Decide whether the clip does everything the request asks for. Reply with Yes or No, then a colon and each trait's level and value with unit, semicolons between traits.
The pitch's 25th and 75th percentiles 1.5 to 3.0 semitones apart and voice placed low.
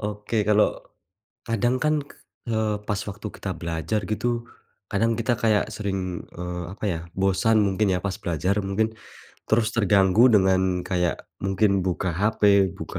Yes: narrow, 2.6 semitones; low, 100 Hz